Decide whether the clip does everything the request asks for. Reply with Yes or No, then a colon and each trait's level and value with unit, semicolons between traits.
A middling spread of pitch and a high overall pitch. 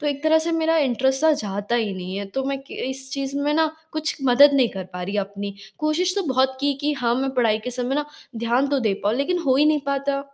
Yes: average, 3.9 semitones; very high, 270 Hz